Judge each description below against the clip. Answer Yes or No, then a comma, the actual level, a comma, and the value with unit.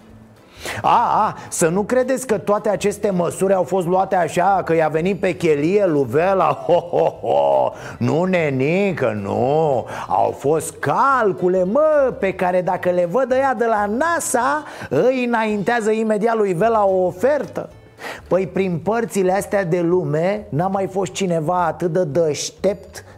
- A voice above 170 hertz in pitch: Yes, high, 190 Hz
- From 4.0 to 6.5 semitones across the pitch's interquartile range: No, average, 3.5 semitones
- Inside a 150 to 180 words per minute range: Yes, average, 155 wpm